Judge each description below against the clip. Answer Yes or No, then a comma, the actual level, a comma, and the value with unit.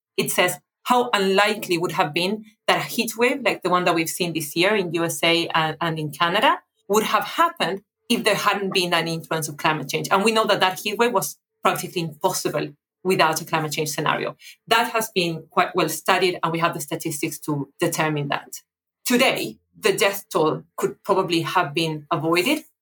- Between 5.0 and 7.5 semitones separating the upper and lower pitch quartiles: No, average, 4.0 semitones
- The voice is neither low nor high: Yes, medium, 180 Hz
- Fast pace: No, average, 190 wpm